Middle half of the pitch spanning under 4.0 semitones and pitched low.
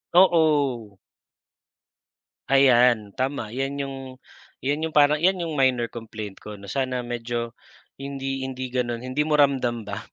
Yes: average, 2.9 semitones; low, 130 Hz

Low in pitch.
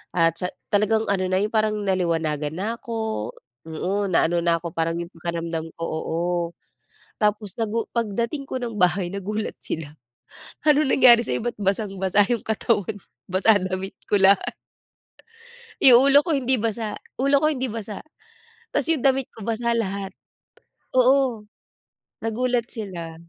No: high, 210 Hz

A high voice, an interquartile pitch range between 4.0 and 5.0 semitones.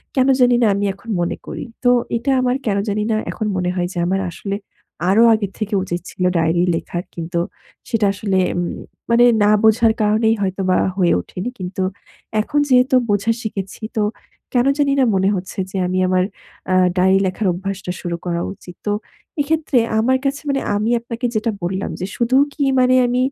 Yes: high, 205 Hz; average, 4.3 semitones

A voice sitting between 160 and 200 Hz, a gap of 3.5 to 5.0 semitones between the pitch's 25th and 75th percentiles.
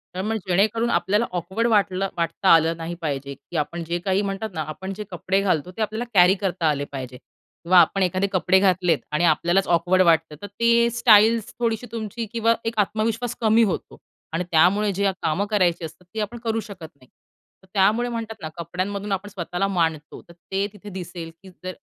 Yes: high, 190 Hz; average, 3.9 semitones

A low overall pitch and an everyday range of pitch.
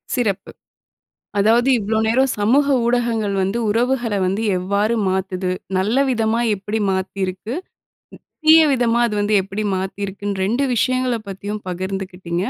No: high, 210 Hz; average, 3.6 semitones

